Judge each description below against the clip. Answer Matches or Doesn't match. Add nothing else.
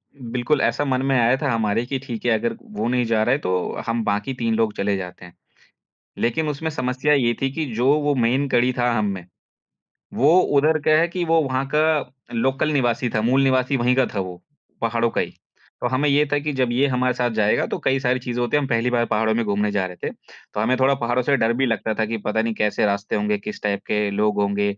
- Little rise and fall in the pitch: Doesn't match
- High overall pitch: Doesn't match